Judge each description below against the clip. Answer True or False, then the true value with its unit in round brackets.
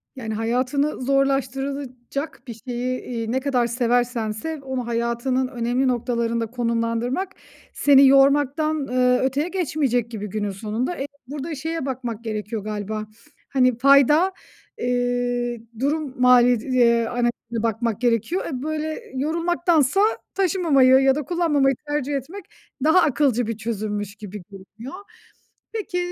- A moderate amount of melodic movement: True (3.3 semitones)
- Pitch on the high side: True (255 Hz)